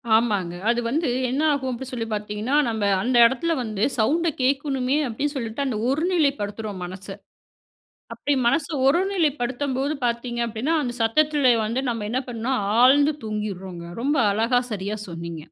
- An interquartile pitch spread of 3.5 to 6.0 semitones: Yes, average, 4.7 semitones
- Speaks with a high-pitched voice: Yes, high, 245 Hz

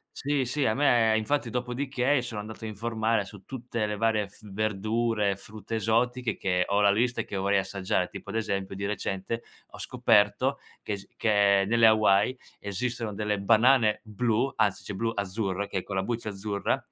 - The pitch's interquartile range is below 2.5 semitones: No, average, 2.8 semitones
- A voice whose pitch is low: Yes, low, 110 Hz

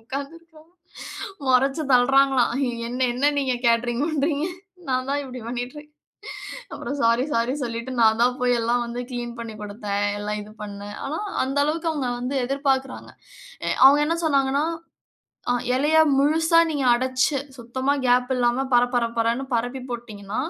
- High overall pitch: Yes, very high, 255 Hz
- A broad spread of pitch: No, average, 2.9 semitones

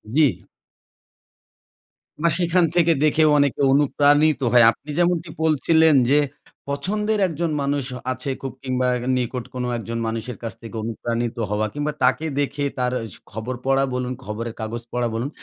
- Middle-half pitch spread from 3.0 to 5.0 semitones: Yes, average, 4.4 semitones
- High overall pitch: No, low, 135 Hz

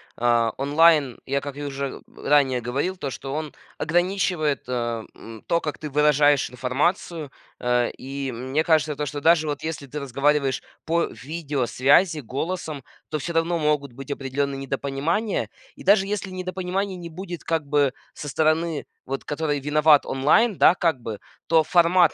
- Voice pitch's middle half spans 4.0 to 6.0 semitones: No, average, 3.5 semitones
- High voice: No, medium, 150 Hz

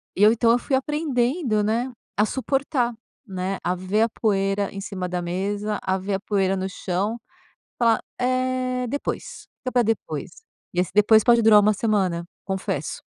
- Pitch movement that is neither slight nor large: Yes, average, 4.1 semitones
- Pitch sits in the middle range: No, high, 215 Hz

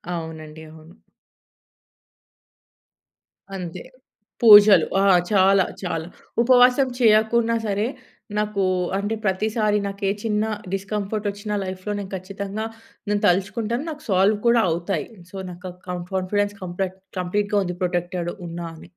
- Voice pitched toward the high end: Yes, high, 200 Hz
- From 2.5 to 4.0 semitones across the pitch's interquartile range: Yes, average, 2.9 semitones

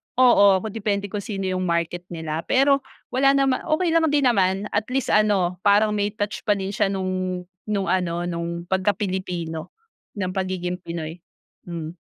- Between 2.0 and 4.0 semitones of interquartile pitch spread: Yes, average, 3.1 semitones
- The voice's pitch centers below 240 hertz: Yes, high, 190 Hz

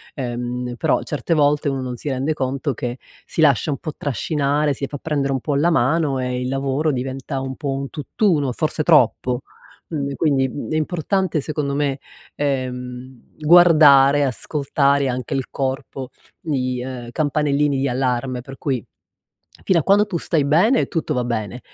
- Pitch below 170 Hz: Yes, medium, 140 Hz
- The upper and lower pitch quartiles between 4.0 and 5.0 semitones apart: No, average, 2.8 semitones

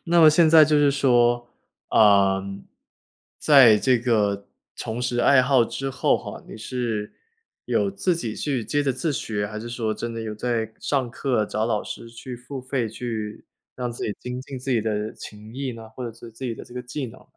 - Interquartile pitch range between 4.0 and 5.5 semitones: No, average, 3.3 semitones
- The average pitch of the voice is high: No, low, 120 Hz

